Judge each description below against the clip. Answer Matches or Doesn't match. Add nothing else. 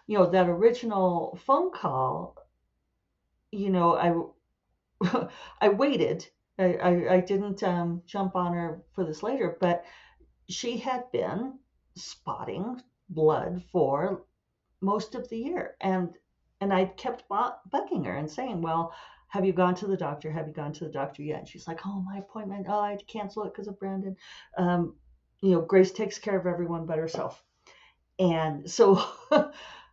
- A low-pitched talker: Doesn't match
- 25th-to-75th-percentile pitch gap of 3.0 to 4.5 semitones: Matches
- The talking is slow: Doesn't match